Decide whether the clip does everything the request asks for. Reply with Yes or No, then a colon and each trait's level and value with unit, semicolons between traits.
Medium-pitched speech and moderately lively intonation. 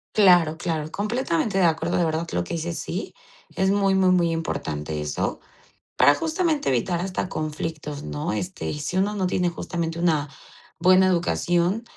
Yes: medium, 170 Hz; average, 3.2 semitones